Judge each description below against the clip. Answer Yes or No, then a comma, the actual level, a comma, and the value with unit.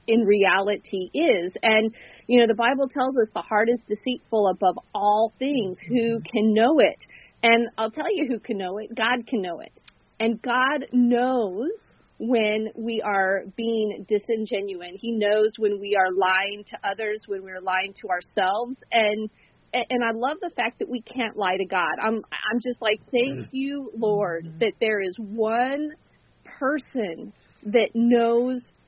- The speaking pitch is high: Yes, high, 225 Hz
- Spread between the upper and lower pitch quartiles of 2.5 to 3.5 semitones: Yes, average, 3.0 semitones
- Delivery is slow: No, average, 165 wpm